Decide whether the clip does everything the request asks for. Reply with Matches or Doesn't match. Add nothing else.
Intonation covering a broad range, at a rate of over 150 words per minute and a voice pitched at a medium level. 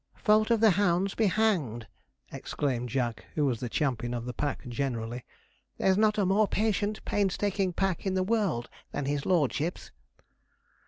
Matches